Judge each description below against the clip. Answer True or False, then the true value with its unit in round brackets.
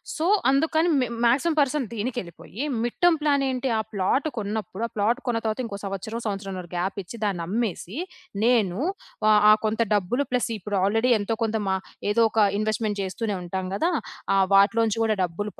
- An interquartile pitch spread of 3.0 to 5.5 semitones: True (3.7 semitones)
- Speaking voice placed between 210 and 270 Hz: True (215 Hz)